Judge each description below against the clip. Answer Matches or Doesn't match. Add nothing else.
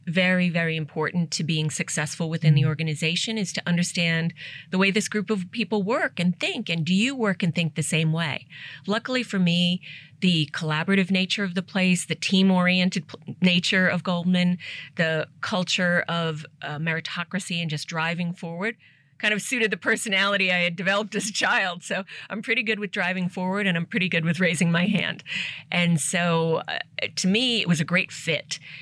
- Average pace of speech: Matches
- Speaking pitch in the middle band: Matches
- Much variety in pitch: Doesn't match